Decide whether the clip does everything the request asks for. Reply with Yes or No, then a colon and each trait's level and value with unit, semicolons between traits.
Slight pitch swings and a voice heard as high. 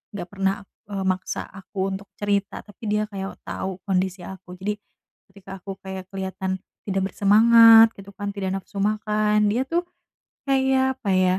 Yes: narrow, 1.9 semitones; high, 200 Hz